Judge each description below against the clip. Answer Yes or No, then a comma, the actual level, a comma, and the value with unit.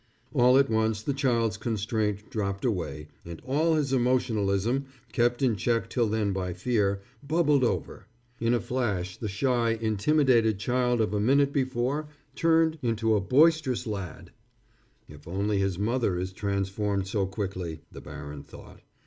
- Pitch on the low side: Yes, low, 110 Hz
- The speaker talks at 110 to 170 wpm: Yes, average, 150 wpm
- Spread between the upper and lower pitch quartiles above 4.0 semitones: Yes, average, 4.6 semitones